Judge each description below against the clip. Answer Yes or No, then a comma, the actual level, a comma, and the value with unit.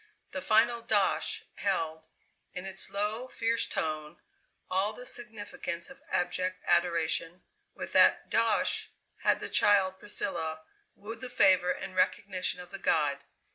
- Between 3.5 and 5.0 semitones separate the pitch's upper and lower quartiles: Yes, average, 4.1 semitones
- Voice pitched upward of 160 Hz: Yes, high, 190 Hz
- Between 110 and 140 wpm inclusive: Yes, slow, 135 wpm